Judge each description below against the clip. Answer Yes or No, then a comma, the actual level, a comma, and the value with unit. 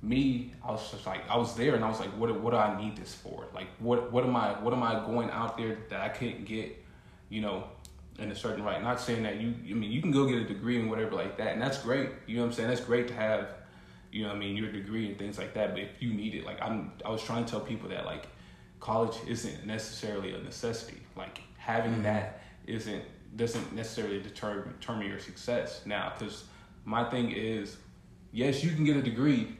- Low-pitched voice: Yes, low, 110 Hz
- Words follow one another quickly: Yes, fast, 245 wpm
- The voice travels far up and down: No, narrow, 2.5 semitones